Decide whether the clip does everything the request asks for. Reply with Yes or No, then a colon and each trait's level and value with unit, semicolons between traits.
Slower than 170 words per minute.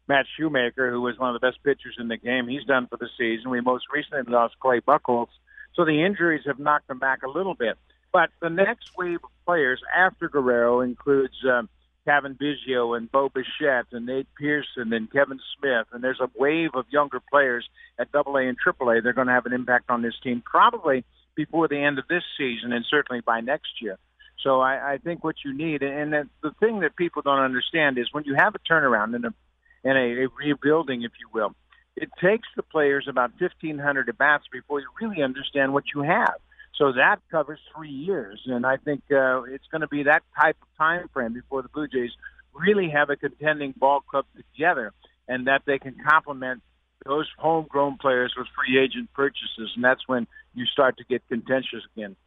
No: fast, 205 wpm